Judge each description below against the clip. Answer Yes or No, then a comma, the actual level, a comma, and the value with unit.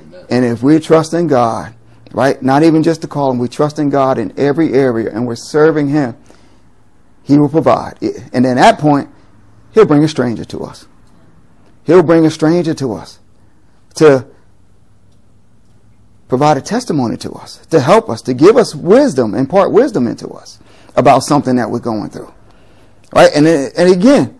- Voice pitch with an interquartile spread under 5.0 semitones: No, wide, 5.4 semitones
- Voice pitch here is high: No, low, 135 Hz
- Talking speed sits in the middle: Yes, average, 175 wpm